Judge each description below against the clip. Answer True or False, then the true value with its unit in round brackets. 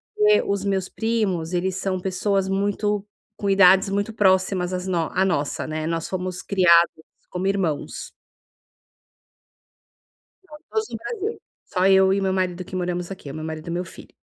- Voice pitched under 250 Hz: True (185 Hz)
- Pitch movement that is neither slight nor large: False (2.0 semitones)